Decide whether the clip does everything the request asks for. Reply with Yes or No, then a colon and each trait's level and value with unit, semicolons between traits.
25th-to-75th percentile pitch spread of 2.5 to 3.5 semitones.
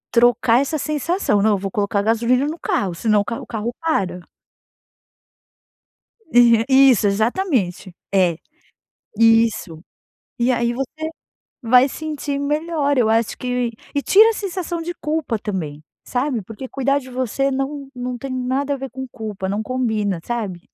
No: average, 4.7 semitones